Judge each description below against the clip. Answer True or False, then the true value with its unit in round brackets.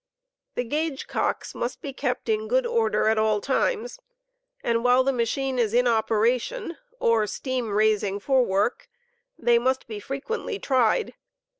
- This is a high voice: True (250 Hz)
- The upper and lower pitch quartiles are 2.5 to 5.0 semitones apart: True (4.7 semitones)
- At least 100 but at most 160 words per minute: True (155 wpm)